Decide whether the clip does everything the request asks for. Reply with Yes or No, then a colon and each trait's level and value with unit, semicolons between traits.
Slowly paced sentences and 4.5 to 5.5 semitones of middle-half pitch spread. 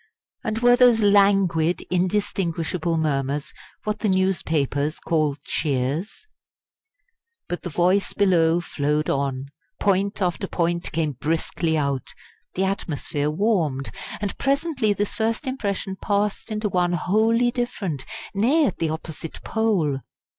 Yes: slow, 120 wpm; average, 5.1 semitones